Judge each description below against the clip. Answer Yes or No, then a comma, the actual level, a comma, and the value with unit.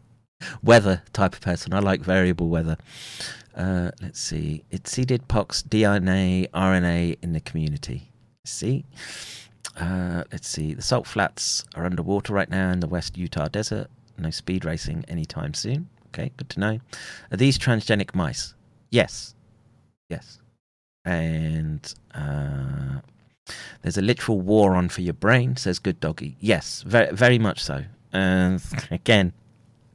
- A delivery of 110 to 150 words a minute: Yes, average, 140 wpm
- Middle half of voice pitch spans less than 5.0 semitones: No, average, 5.3 semitones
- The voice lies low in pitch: Yes, very low, 95 Hz